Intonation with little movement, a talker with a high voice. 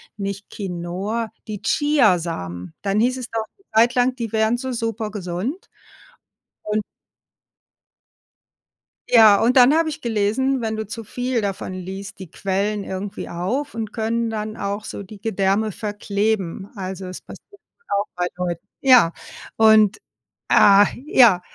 No: average, 3.2 semitones; high, 215 Hz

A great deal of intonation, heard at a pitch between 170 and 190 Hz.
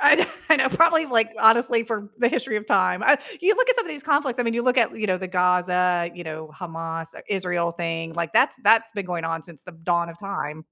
Yes: wide, 5.8 semitones; medium, 185 Hz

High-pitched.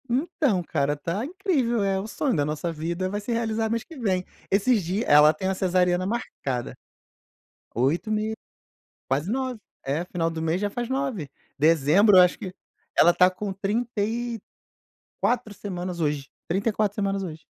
Yes: high, 195 Hz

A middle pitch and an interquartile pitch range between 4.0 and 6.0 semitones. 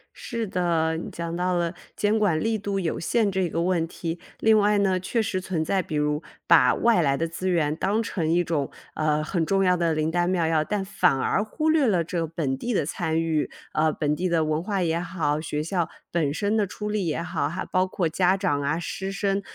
No: medium, 175 Hz; average, 3.5 semitones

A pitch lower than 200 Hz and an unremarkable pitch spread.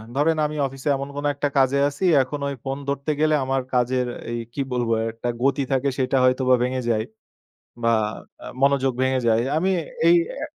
No: low, 135 Hz; narrow, 1.9 semitones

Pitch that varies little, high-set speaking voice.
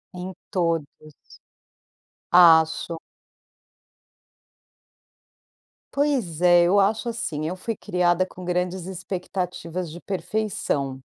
No: narrow, 2.2 semitones; medium, 180 Hz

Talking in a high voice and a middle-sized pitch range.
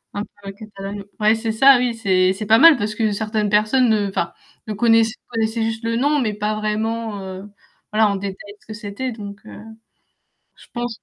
No: high, 215 Hz; narrow, 2.0 semitones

